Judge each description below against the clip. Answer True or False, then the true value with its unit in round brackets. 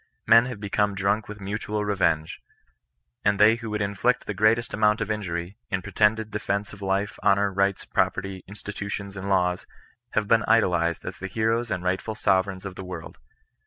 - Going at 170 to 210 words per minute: True (180 wpm)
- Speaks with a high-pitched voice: False (100 Hz)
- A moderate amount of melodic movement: False (2.0 semitones)